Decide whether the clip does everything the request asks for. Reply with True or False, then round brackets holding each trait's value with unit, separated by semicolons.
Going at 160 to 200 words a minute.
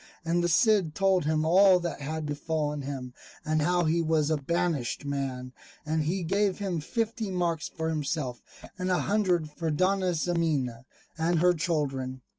True (165 wpm)